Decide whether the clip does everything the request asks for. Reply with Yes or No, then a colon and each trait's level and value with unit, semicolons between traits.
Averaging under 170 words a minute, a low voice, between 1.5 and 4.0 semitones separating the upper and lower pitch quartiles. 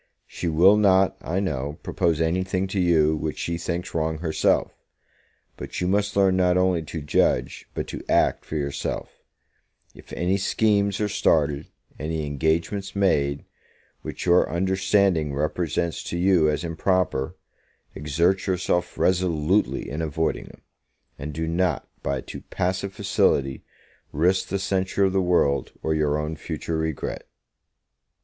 Yes: average, 145 wpm; very low, 85 Hz; average, 3.4 semitones